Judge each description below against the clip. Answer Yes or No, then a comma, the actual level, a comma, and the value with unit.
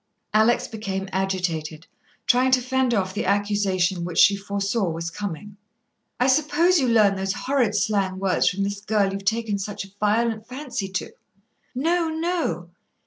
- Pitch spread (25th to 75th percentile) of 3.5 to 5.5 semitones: Yes, average, 4.0 semitones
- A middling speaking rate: Yes, average, 155 wpm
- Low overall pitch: No, high, 205 Hz